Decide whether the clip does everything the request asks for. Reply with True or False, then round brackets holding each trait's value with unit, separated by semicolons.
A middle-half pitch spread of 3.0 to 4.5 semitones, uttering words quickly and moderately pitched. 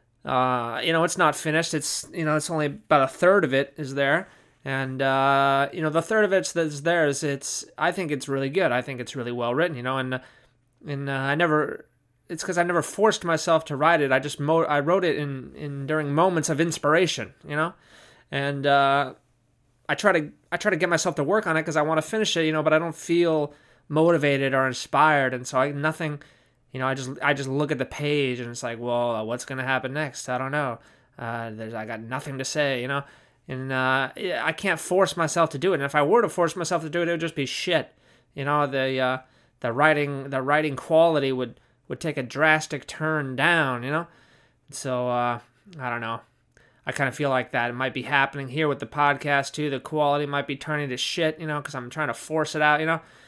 True (3.4 semitones; 240 wpm; 145 Hz)